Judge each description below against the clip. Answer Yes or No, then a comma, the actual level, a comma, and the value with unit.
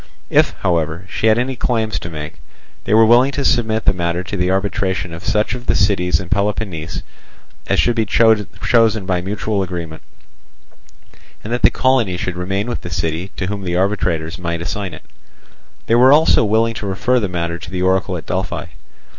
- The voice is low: Yes, very low, 95 Hz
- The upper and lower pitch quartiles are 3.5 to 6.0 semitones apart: Yes, average, 4.0 semitones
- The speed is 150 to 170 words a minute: No, average, 190 wpm